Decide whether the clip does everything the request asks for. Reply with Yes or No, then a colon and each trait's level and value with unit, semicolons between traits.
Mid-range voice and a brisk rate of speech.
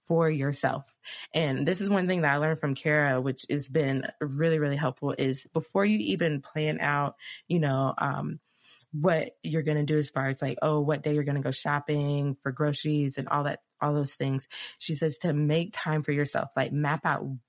Yes: medium, 150 Hz; fast, 215 wpm